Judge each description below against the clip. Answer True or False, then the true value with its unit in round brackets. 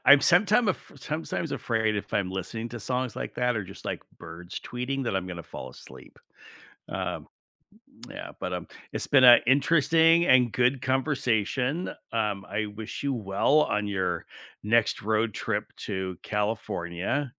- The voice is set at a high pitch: False (115 Hz)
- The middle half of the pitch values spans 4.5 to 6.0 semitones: True (5.2 semitones)